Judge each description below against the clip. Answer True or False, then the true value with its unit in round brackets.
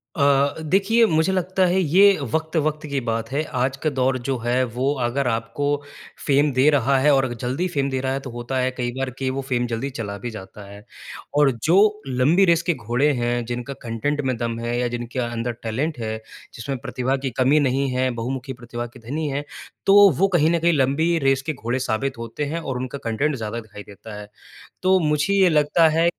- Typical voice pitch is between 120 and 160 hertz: True (135 Hz)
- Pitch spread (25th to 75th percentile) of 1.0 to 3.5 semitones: False (4.0 semitones)